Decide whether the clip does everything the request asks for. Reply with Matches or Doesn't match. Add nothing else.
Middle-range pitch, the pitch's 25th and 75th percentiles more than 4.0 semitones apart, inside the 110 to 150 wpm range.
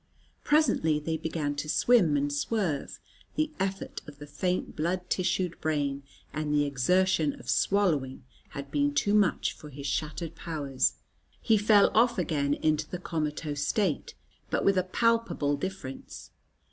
Matches